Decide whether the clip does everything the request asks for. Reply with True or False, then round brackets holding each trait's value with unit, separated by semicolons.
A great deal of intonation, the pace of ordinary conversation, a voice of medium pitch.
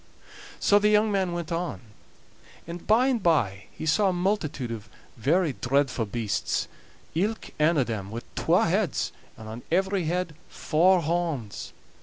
True (7.2 semitones; 155 wpm; 165 Hz)